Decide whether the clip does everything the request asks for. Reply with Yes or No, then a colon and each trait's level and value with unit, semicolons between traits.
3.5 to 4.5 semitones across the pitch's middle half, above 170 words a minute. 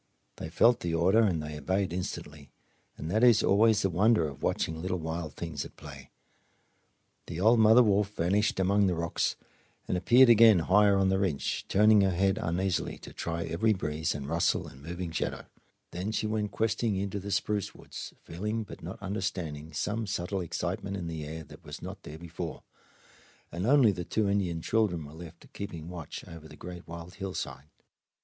Yes: average, 3.9 semitones; average, 185 wpm